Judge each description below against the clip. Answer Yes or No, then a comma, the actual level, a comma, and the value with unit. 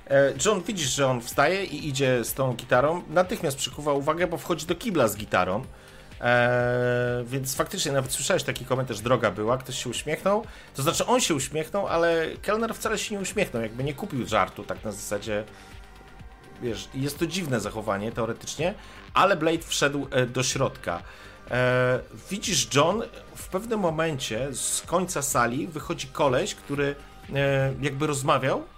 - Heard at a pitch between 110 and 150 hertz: Yes, low, 135 Hz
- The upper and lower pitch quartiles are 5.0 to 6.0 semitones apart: Yes, average, 5.3 semitones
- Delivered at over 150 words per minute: Yes, fast, 160 wpm